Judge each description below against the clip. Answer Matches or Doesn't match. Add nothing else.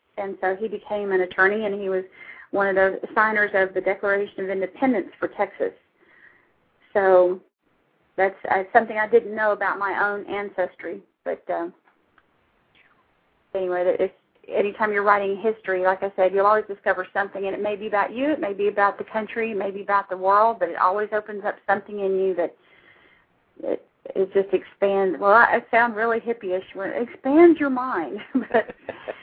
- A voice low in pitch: Doesn't match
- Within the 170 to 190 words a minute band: Matches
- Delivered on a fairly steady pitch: Matches